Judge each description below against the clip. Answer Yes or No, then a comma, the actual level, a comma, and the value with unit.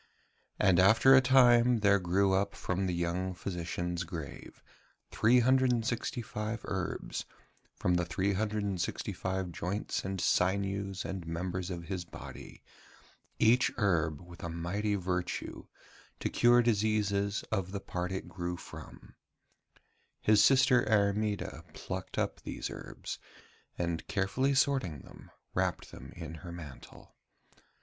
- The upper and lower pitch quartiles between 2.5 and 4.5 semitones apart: Yes, average, 3.5 semitones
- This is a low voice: Yes, very low, 95 Hz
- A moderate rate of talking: No, slow, 120 wpm